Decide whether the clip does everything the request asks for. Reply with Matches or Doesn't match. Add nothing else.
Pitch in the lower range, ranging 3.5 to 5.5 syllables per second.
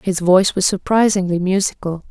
Doesn't match